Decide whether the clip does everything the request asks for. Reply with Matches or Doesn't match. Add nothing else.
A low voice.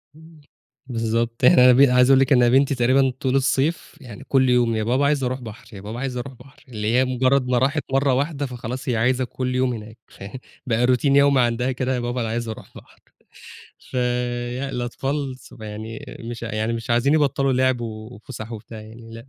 Matches